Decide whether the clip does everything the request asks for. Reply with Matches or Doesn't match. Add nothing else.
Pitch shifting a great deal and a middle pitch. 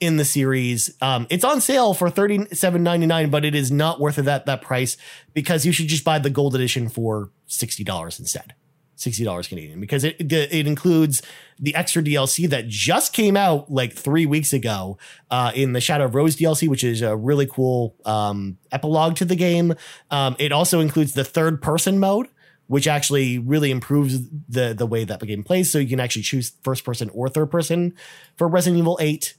Doesn't match